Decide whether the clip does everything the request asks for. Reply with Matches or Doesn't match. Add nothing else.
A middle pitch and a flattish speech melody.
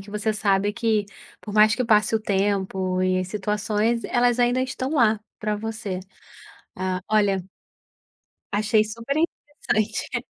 Doesn't match